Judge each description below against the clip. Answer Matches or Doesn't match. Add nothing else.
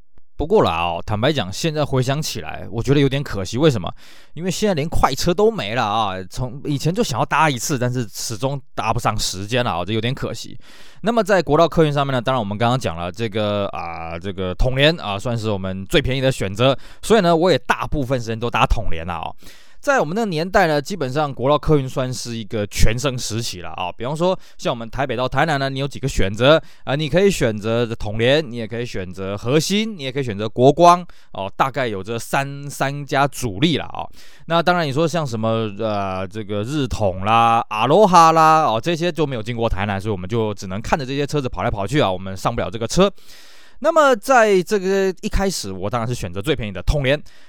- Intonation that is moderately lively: Doesn't match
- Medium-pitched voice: Doesn't match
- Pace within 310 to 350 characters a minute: Matches